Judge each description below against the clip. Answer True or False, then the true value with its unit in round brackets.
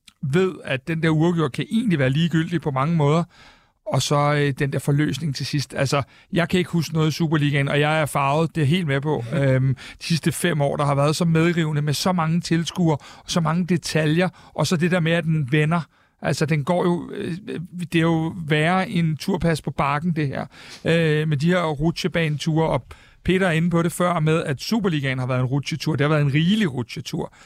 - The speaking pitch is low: False (160 Hz)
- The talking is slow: False (225 wpm)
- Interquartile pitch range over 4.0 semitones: False (2.8 semitones)